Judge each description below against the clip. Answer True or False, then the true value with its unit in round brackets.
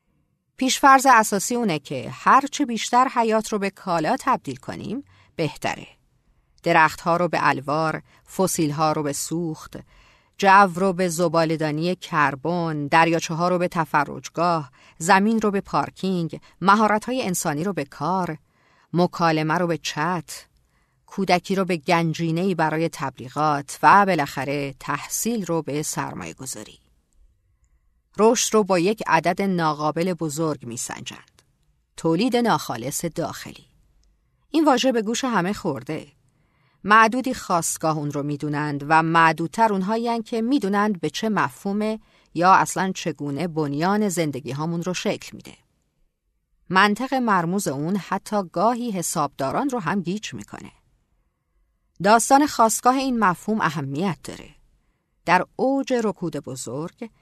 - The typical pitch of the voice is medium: True (170 Hz)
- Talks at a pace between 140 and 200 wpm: False (125 wpm)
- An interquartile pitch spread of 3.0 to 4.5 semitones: False (5.2 semitones)